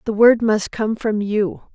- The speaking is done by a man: No, female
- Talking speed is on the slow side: No, fast, 205 wpm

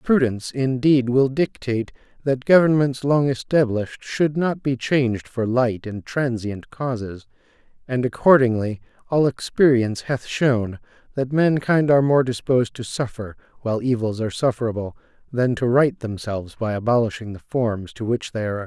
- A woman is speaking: No, male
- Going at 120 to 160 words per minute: Yes, average, 150 wpm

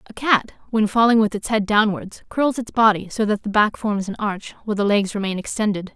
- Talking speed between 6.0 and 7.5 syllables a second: No, 5.6 syllables/s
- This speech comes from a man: No, female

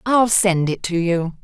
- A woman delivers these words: Yes, female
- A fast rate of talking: Yes, fast, 210 wpm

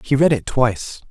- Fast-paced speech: Yes, fast, 220 wpm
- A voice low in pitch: Yes, low, 125 Hz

